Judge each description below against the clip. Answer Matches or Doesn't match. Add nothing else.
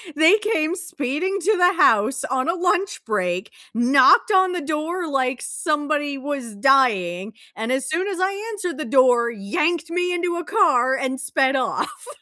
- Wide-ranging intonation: Matches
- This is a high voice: Matches